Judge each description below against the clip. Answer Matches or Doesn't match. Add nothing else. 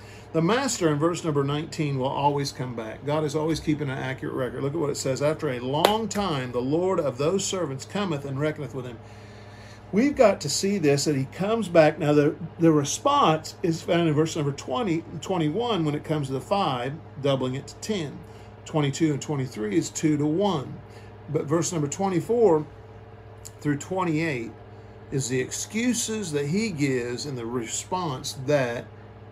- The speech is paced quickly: Doesn't match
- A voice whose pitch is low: Doesn't match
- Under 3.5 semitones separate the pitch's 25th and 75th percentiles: Doesn't match